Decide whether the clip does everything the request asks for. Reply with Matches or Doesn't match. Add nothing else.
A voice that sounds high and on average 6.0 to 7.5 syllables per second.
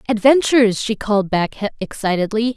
Doesn't match